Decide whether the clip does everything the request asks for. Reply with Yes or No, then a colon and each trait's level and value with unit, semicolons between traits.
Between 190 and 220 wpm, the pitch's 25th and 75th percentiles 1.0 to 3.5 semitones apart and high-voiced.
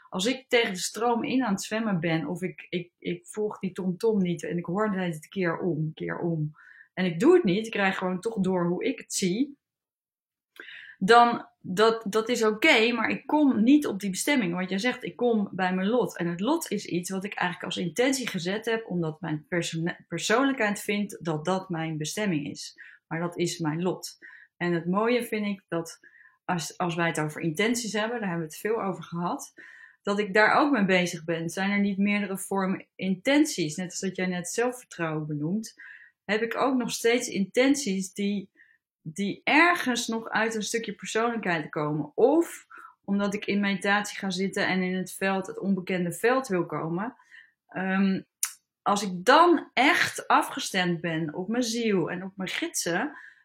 No: average, 195 wpm; average, 4.4 semitones; high, 195 Hz